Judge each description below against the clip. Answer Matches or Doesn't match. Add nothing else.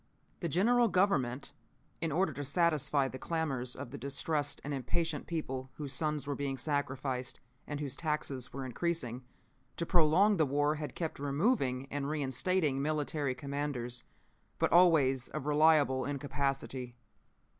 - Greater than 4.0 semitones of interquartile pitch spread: Doesn't match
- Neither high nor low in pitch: Matches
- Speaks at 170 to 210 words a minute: Doesn't match